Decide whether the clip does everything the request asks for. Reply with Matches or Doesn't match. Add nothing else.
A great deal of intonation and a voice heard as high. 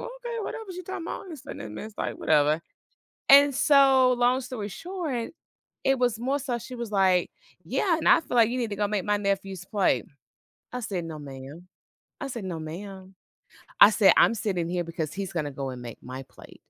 Matches